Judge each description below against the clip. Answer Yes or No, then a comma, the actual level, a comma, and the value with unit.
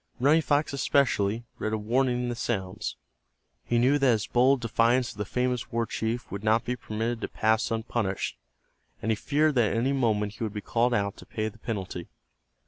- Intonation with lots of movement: No, narrow, 2.5 semitones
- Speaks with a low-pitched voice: Yes, low, 115 Hz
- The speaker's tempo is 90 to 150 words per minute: No, fast, 205 wpm